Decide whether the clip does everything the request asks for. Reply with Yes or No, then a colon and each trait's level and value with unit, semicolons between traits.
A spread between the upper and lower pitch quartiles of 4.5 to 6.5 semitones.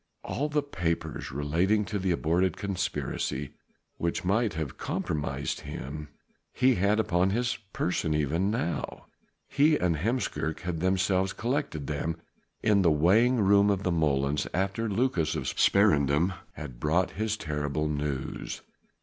Yes: average, 5.1 semitones